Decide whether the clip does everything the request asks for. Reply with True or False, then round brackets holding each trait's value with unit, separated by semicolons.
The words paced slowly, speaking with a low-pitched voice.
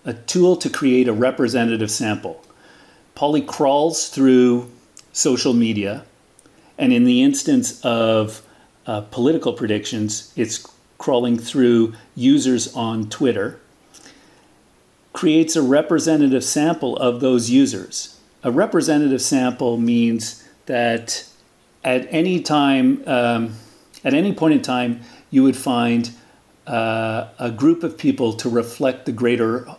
True (120 wpm; 125 Hz)